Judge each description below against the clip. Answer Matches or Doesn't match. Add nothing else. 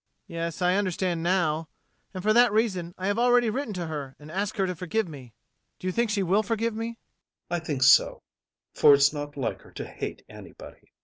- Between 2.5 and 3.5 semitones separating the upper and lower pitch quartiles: Doesn't match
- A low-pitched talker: Doesn't match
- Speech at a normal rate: Doesn't match